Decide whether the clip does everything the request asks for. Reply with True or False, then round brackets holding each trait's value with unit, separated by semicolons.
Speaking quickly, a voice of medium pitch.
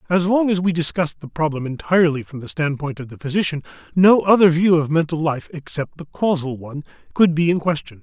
True (210 wpm; 160 Hz)